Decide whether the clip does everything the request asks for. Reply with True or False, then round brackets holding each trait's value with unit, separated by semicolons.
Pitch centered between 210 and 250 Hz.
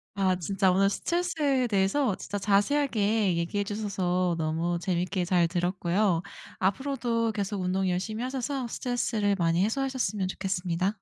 False (195 Hz)